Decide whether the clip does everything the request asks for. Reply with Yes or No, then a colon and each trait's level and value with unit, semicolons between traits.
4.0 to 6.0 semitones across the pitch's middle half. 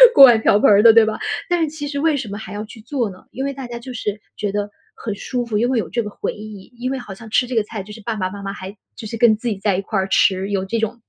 No: average, 3.1 semitones